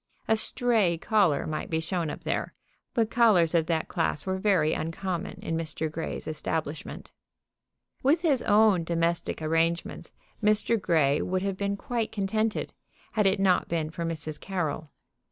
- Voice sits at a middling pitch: Yes, medium, 175 Hz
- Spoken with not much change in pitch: No, average, 4.6 semitones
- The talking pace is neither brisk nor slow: Yes, average, 155 wpm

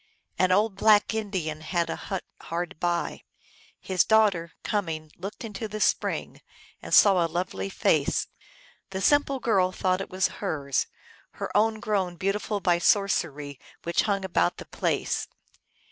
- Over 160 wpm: No, average, 145 wpm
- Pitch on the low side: No, high, 190 Hz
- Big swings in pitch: No, average, 3.5 semitones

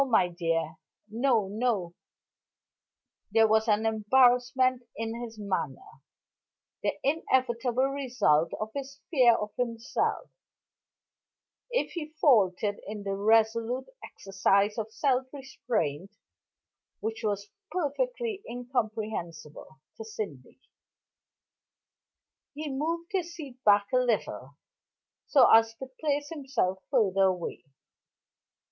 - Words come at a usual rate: No, slow, 105 wpm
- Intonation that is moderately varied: Yes, average, 4.6 semitones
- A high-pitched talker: Yes, high, 225 Hz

